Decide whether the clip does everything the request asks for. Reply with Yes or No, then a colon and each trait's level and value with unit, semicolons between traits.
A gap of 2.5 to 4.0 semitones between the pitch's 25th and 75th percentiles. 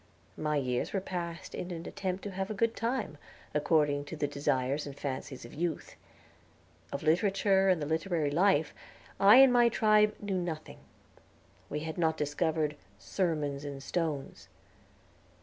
No: average, 4.8 semitones